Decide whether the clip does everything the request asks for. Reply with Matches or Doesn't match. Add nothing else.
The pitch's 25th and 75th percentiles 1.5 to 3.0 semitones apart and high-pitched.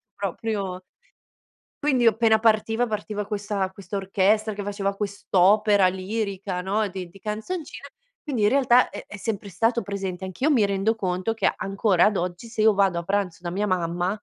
Matches